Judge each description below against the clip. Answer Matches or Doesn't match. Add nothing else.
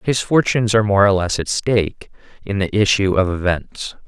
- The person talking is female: Doesn't match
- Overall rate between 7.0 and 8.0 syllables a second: Doesn't match